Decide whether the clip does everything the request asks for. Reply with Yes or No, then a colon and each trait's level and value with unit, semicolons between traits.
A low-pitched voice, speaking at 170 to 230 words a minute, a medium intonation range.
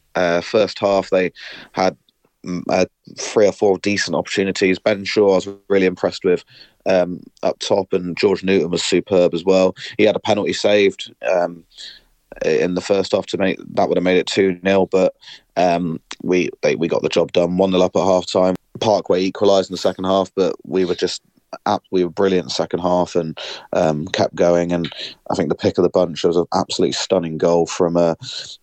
No: very low, 90 Hz; fast, 205 wpm; narrow, 1.7 semitones